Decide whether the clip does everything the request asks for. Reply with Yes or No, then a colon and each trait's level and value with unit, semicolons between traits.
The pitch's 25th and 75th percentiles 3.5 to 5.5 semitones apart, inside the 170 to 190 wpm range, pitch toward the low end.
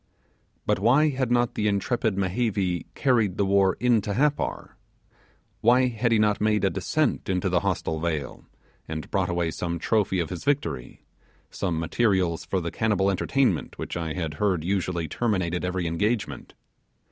No: average, 4.6 semitones; average, 160 wpm; very low, 95 Hz